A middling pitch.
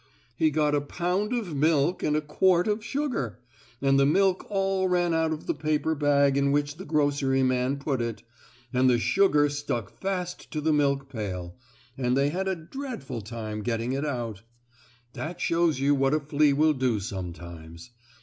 Yes: medium, 145 Hz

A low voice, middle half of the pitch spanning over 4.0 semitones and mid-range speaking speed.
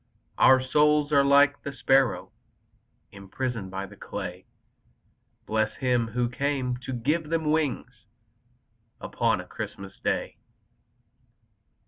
No: low, 130 Hz; average, 4.7 semitones; slow, 110 wpm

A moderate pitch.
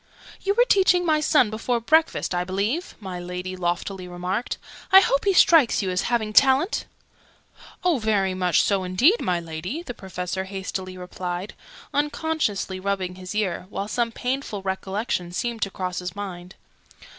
No: high, 195 Hz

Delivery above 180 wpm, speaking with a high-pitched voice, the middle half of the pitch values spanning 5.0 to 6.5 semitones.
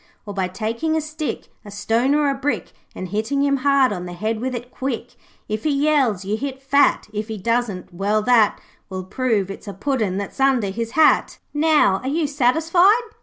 Yes: average, 200 wpm; high, 240 Hz; wide, 5.4 semitones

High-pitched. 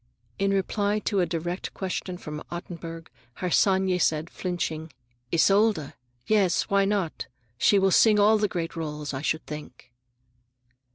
No: medium, 180 Hz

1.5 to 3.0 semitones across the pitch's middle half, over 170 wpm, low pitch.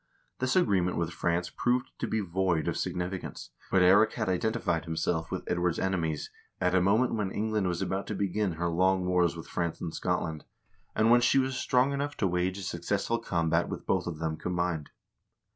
No: average, 3.4 semitones; average, 195 wpm; very low, 90 Hz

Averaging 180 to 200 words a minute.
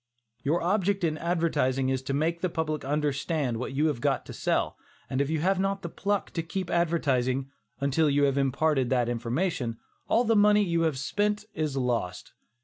Yes: average, 190 wpm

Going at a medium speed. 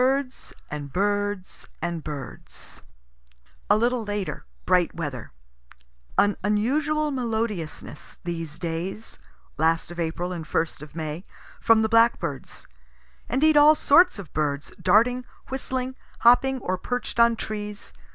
No: slow, 120 wpm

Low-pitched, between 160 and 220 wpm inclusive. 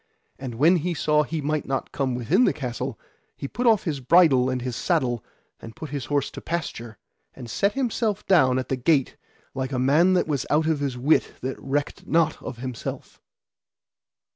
No: medium, 145 Hz; average, 190 wpm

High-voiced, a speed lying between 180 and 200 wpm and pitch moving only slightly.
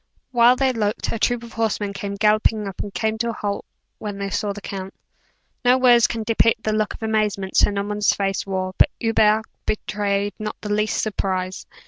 Yes: high, 210 Hz; average, 195 wpm; narrow, 2.0 semitones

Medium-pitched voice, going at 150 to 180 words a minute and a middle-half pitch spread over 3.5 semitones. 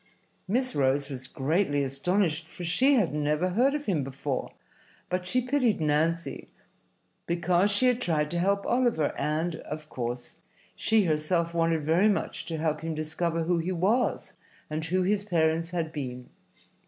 Yes: medium, 165 Hz; average, 160 wpm; average, 4.2 semitones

